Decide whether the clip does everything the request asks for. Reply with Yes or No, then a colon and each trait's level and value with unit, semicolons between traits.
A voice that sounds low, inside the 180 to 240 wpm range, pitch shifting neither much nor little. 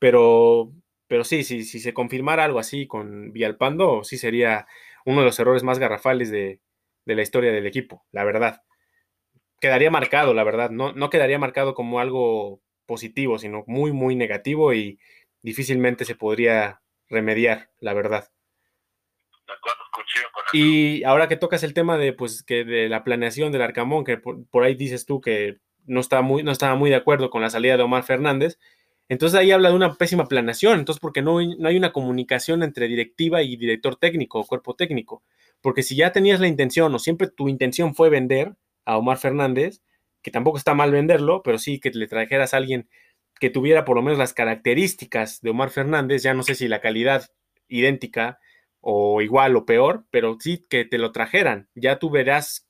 Yes: low, 130 Hz; average, 185 wpm; average, 4.1 semitones